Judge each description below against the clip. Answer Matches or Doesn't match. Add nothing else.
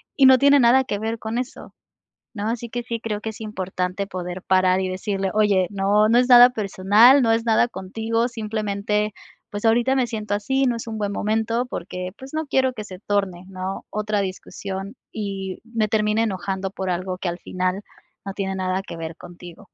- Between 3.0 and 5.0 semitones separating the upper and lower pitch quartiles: Matches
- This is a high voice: Matches